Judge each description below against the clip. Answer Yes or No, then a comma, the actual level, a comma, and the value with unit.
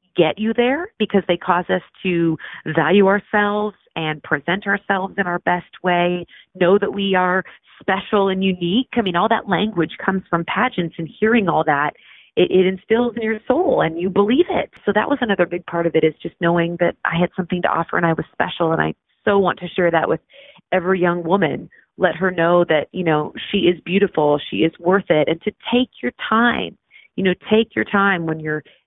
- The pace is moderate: No, fast, 215 wpm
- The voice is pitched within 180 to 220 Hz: Yes, medium, 185 Hz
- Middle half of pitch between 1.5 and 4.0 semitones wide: Yes, average, 3.0 semitones